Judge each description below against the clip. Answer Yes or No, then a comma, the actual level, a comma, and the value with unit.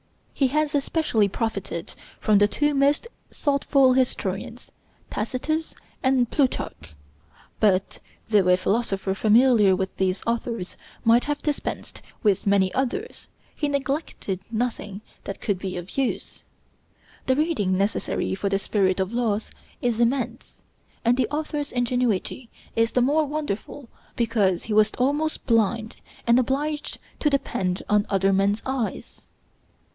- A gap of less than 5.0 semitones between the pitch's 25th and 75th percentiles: No, wide, 5.5 semitones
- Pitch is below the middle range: No, high, 230 Hz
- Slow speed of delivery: Yes, slow, 130 wpm